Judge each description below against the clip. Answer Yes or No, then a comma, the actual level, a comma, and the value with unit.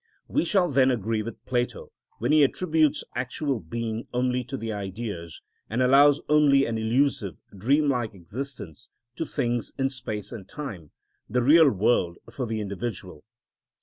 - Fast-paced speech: No, average, 150 wpm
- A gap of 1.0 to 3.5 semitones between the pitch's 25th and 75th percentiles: No, average, 4.5 semitones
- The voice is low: Yes, low, 120 Hz